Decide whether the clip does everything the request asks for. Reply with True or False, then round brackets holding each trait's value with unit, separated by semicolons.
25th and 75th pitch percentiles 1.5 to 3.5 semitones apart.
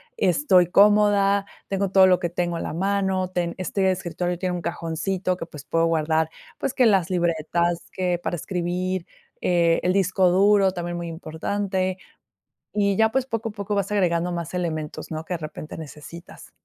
True (2.4 semitones)